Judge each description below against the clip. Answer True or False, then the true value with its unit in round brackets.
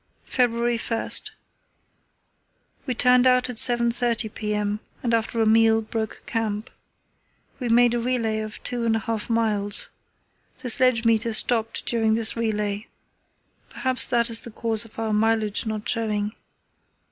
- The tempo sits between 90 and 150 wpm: True (140 wpm)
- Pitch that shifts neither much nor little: False (1.5 semitones)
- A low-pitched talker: False (225 Hz)